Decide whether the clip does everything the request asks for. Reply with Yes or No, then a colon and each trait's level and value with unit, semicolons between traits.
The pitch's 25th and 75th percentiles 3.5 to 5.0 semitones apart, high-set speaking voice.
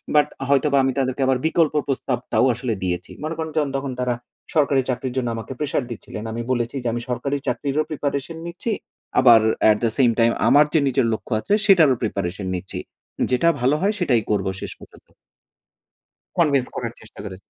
No: average, 3.8 semitones; low, 130 Hz